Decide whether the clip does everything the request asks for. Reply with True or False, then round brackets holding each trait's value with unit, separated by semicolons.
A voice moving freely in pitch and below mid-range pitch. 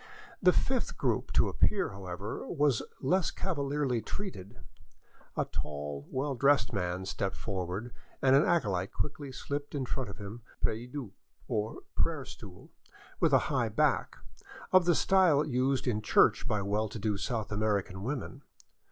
True (6.4 semitones; 120 Hz)